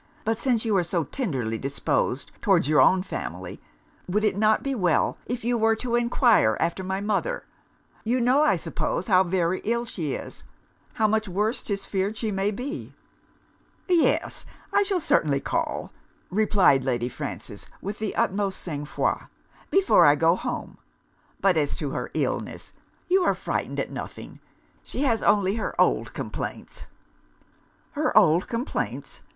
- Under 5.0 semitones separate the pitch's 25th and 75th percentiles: No, wide, 5.5 semitones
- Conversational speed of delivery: Yes, average, 155 wpm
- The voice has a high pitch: Yes, high, 205 Hz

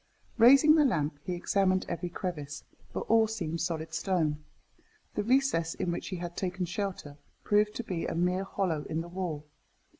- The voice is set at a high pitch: No, medium, 180 Hz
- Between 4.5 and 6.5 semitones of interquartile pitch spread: No, average, 3.6 semitones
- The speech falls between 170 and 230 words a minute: Yes, average, 175 wpm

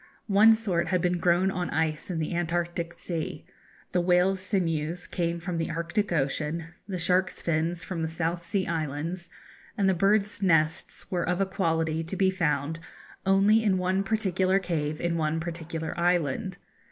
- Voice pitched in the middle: Yes, medium, 175 Hz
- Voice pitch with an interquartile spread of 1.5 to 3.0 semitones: Yes, narrow, 2.5 semitones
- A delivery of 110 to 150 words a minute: No, average, 165 wpm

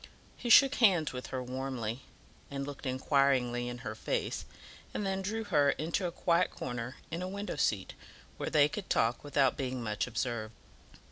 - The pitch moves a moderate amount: No, wide, 6.2 semitones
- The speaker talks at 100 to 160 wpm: No, average, 175 wpm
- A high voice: No, low, 135 Hz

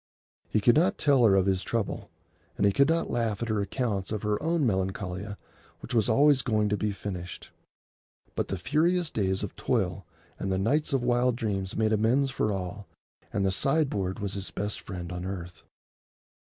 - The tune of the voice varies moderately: Yes, average, 4.7 semitones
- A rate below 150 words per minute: No, average, 190 wpm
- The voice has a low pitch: Yes, low, 105 Hz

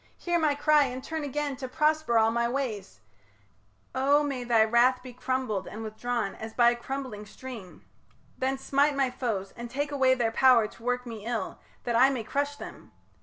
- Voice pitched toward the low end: No, very high, 250 Hz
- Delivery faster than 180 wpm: Yes, average, 190 wpm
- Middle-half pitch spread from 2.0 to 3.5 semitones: Yes, average, 3.2 semitones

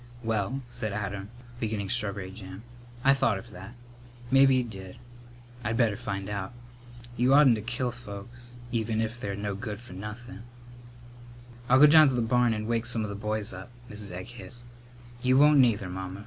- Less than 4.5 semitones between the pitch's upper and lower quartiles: Yes, average, 3.4 semitones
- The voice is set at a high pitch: No, low, 110 Hz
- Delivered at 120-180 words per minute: Yes, average, 175 wpm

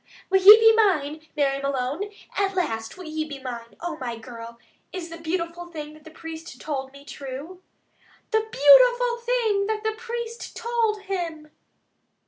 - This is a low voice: No, very high, 330 Hz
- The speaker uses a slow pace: No, average, 160 wpm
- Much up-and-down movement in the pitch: Yes, wide, 7.0 semitones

